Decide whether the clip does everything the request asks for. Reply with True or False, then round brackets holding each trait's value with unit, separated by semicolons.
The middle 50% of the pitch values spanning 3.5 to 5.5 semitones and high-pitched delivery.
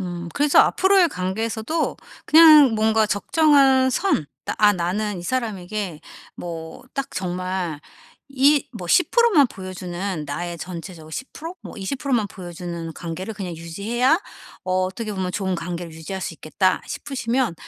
False (6.7 semitones; 195 Hz)